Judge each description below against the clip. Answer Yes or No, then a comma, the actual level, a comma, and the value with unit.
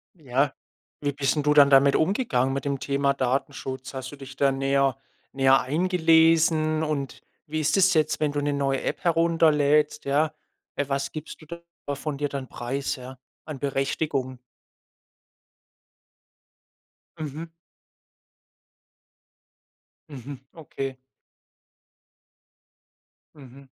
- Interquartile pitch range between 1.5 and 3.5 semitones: Yes, narrow, 2.4 semitones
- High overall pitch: No, medium, 140 Hz